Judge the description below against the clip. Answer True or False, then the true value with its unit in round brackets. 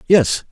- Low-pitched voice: False (155 Hz)